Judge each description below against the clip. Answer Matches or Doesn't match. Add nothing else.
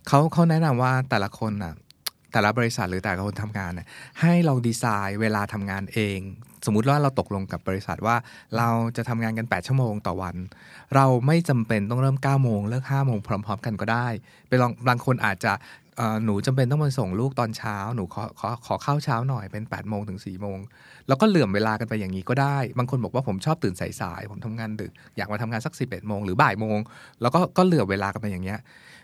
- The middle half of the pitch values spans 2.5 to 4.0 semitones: Doesn't match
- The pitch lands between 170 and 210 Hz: Doesn't match